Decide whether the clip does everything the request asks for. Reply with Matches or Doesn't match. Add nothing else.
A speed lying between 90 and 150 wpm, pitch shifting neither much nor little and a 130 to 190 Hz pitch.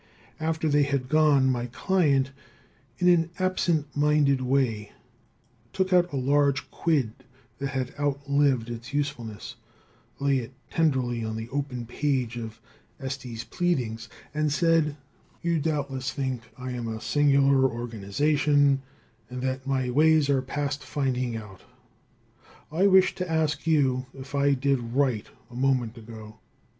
Matches